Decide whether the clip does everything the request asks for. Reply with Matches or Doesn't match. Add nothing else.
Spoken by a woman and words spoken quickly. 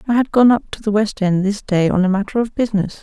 Matches